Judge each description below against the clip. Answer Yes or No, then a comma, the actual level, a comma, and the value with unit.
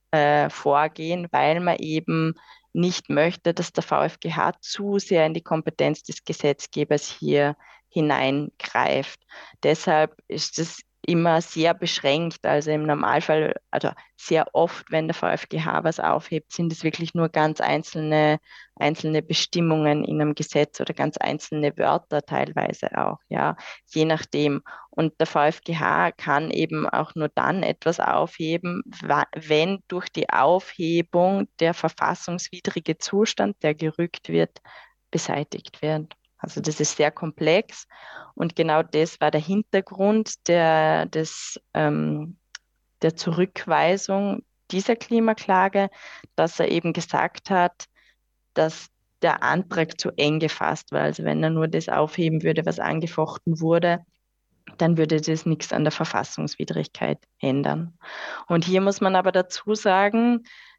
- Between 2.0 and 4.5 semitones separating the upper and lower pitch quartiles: Yes, narrow, 2.5 semitones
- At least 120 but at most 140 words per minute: Yes, average, 130 wpm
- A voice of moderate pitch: Yes, medium, 160 Hz